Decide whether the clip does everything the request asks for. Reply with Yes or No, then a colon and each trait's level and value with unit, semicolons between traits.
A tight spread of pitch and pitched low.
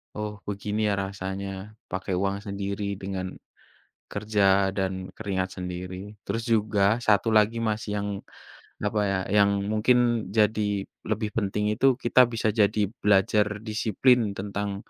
Yes: narrow, 1.6 semitones; low, 105 Hz